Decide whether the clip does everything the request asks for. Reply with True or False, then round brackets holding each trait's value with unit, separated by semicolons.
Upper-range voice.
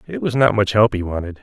False (100 Hz)